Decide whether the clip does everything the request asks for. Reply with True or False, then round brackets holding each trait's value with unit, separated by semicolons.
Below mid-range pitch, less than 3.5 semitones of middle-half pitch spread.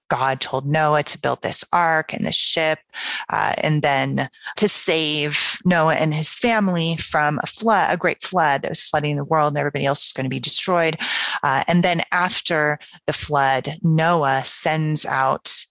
False (155 Hz; 2.9 semitones)